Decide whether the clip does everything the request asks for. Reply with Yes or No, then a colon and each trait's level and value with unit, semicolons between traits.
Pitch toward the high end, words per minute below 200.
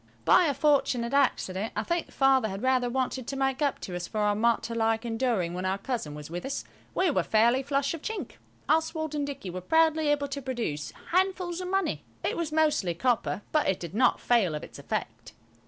No: very high, 255 Hz; fast, 205 wpm